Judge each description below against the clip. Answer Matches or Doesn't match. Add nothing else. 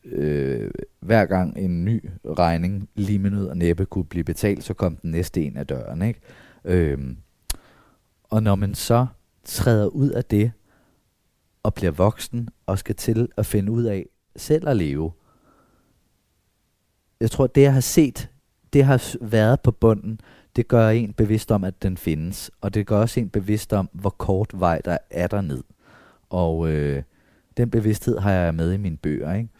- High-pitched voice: Doesn't match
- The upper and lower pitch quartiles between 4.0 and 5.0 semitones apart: Matches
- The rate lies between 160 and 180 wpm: Matches